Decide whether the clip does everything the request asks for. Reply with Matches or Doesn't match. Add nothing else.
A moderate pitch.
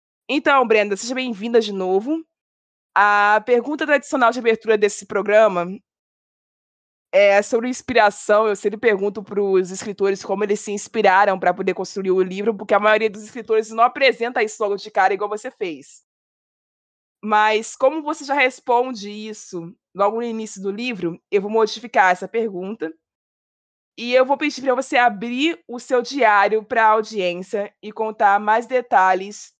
Doesn't match